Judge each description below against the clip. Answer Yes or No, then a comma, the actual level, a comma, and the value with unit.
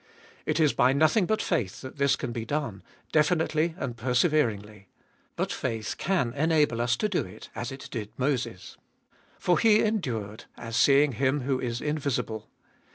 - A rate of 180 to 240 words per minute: No, average, 165 wpm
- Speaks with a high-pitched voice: No, low, 135 Hz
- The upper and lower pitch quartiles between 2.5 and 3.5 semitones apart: No, average, 4.8 semitones